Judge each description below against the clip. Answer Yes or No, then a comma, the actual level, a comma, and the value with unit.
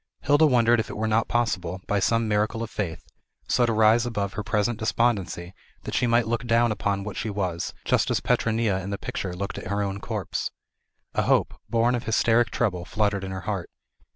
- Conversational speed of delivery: No, fast, 210 wpm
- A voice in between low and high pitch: No, low, 110 Hz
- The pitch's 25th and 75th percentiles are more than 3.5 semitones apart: No, average, 2.8 semitones